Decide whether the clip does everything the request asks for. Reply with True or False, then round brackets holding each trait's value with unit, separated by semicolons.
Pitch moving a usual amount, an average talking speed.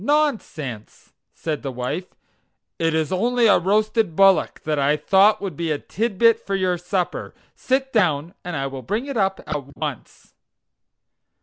False (6.1 semitones; 160 wpm)